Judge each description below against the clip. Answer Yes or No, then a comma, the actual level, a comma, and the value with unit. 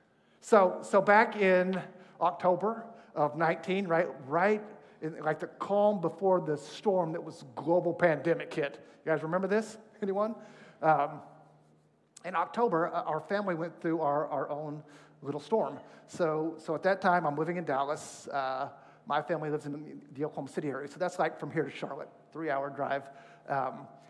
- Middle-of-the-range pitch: Yes, medium, 165 Hz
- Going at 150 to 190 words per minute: Yes, average, 165 wpm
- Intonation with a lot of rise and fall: No, average, 4.2 semitones